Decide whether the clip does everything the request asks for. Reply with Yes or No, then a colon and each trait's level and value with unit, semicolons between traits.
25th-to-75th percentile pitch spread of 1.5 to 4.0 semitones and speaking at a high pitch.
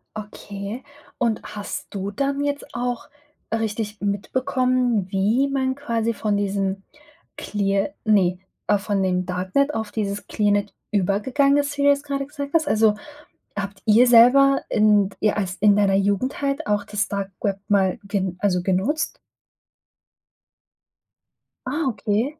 No: average, 4.6 semitones; high, 210 Hz